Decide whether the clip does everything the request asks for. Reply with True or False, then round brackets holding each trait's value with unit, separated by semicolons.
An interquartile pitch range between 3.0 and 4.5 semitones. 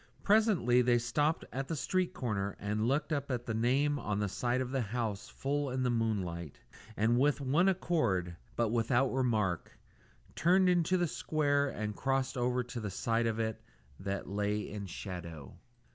False (5.2 semitones)